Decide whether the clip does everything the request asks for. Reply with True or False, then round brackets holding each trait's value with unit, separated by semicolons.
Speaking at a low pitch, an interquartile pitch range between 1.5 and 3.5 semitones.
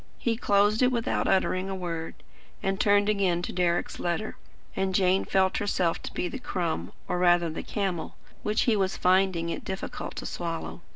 False (190 Hz; 2.7 semitones)